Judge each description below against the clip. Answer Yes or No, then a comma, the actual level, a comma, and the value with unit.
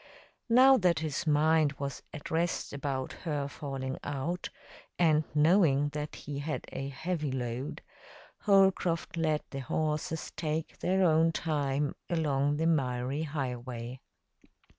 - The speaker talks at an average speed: No, slow, 125 wpm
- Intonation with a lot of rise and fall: No, average, 3.0 semitones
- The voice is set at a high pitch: No, medium, 150 Hz